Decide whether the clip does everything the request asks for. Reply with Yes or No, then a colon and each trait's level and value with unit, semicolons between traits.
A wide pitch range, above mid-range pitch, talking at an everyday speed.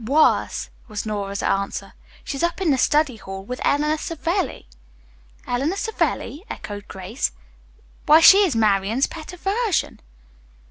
No: wide, 7.9 semitones; very high, 280 Hz; slow, 130 wpm